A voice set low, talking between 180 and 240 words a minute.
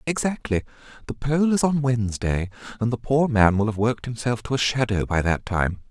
Yes: low, 120 Hz; fast, 205 wpm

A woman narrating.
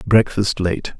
No: male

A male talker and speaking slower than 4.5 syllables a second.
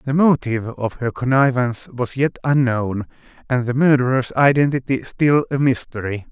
No: male; 5.0 syllables/s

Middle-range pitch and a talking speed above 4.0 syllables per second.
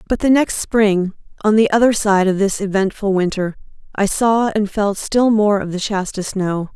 No: high, 205 Hz; 4.6 syllables/s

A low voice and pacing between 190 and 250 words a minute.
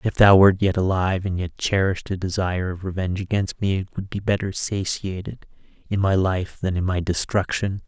Yes: very low, 95 Hz; average, 200 wpm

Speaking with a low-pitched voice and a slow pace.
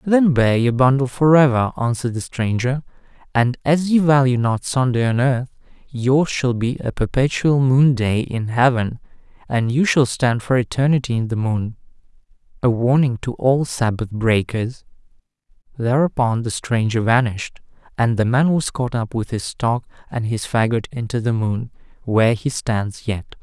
No: low, 125 Hz; average, 160 wpm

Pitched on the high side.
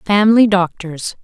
Yes: high, 195 Hz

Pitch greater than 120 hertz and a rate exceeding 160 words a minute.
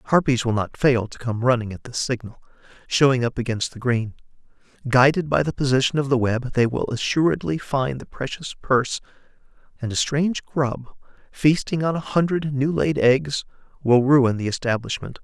Yes: low, 130 Hz; average, 175 wpm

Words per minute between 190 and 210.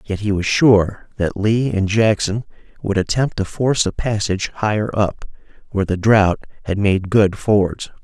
No: average, 170 wpm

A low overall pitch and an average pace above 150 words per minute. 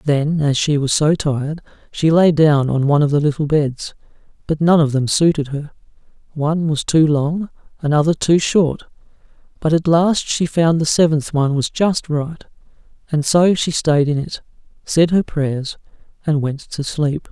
No: medium, 155 Hz; average, 180 wpm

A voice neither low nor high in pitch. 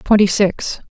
No: high, 200 Hz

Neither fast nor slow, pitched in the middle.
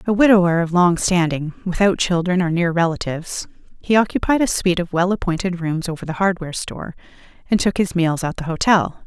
Yes: average, 190 wpm; medium, 180 Hz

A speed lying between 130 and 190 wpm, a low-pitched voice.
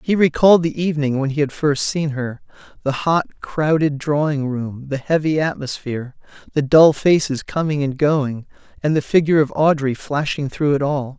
No: average, 170 wpm; medium, 145 Hz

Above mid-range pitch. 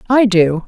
Yes: high, 205 Hz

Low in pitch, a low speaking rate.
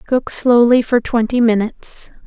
No: high, 235 Hz; slow, 130 wpm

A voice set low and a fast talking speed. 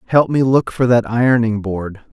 No: low, 115 Hz; average, 190 wpm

